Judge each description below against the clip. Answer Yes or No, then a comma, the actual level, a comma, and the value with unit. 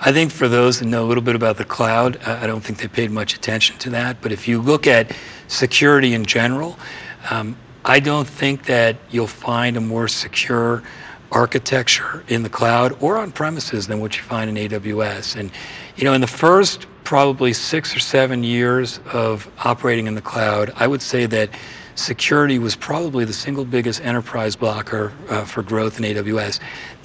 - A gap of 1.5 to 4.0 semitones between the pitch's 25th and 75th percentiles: Yes, average, 3.1 semitones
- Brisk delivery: No, average, 185 wpm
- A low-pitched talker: Yes, low, 120 Hz